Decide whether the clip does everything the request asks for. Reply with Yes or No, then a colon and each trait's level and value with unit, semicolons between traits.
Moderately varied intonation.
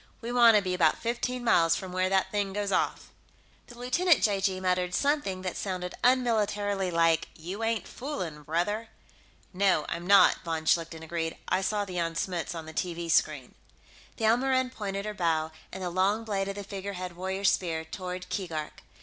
Yes: average, 3.6 semitones